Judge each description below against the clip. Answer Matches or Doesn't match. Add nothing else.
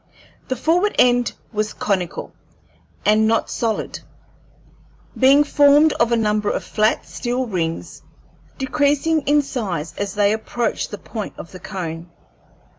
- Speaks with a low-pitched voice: Doesn't match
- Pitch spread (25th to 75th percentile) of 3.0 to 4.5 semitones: Doesn't match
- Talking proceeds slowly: Matches